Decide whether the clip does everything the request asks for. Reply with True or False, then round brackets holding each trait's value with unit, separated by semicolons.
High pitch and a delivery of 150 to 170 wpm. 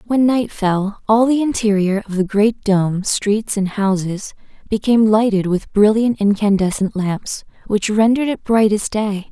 True (210 Hz; 160 wpm)